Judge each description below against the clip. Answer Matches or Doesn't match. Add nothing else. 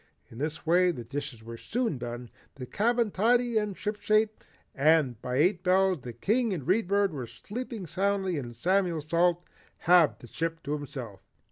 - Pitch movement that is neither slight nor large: Doesn't match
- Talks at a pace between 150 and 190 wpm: Matches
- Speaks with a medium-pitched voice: Matches